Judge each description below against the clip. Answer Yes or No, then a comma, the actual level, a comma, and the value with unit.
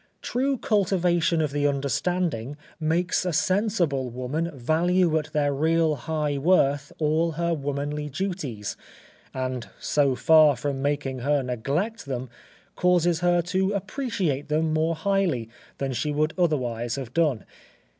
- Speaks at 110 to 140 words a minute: Yes, slow, 135 wpm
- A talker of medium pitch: Yes, medium, 155 Hz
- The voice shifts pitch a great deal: No, average, 4.1 semitones